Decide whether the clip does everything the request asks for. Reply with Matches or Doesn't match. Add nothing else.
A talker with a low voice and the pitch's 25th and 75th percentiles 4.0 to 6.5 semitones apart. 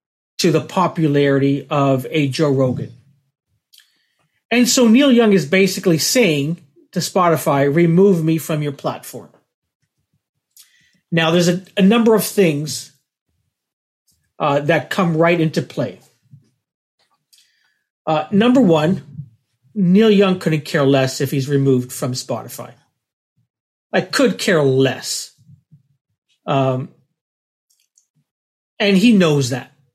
Doesn't match